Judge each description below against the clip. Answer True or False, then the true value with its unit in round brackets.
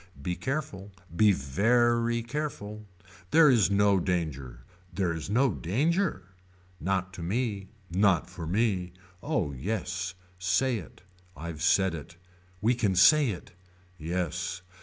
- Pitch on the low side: True (95 Hz)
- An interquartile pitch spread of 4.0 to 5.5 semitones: True (5.1 semitones)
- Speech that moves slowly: True (120 wpm)